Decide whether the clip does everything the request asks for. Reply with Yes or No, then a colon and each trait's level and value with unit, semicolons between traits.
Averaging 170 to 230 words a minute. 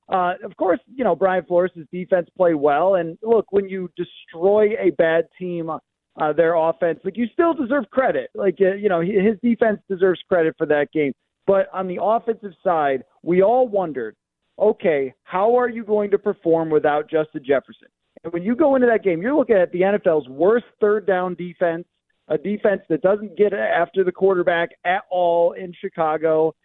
Yes: average, 190 wpm